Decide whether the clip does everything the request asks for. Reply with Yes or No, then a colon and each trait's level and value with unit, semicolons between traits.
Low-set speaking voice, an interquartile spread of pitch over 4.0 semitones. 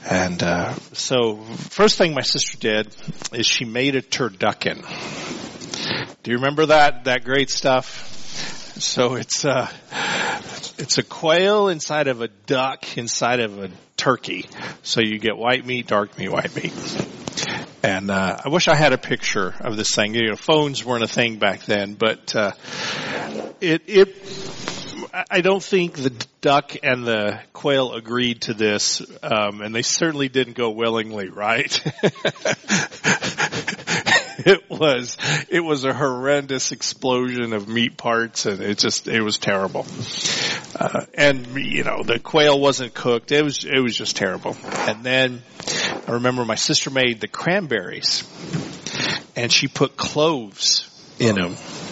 Yes: low, 125 Hz; average, 4.5 semitones